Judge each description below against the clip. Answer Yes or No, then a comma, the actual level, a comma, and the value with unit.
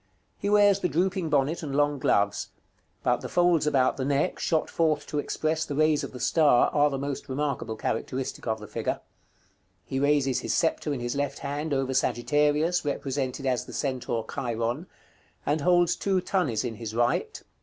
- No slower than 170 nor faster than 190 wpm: Yes, average, 180 wpm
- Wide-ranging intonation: No, average, 3.5 semitones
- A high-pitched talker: No, medium, 145 Hz